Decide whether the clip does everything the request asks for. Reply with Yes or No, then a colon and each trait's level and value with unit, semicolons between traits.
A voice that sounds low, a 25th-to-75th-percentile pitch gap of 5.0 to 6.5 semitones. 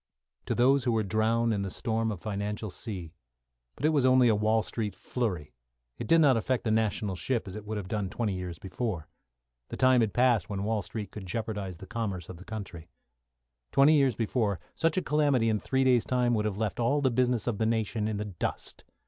No: low, 110 Hz; average, 3.5 semitones